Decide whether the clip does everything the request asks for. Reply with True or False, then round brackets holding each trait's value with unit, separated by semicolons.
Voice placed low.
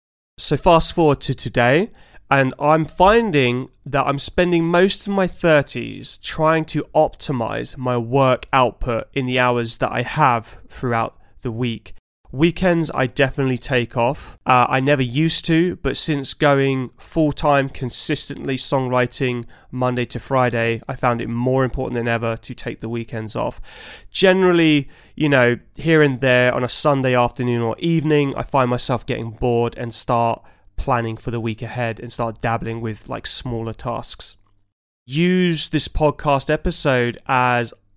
True (130 Hz)